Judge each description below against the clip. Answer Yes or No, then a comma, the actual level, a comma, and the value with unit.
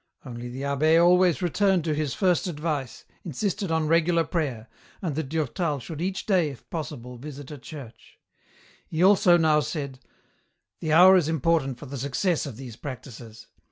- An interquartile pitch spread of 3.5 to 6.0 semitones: Yes, average, 4.2 semitones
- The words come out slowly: No, average, 170 wpm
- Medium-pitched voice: Yes, medium, 155 Hz